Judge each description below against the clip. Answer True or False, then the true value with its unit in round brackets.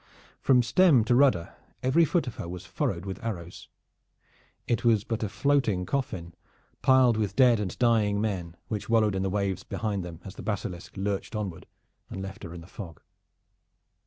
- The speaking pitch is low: True (105 Hz)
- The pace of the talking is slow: False (180 wpm)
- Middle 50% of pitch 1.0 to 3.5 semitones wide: False (4.2 semitones)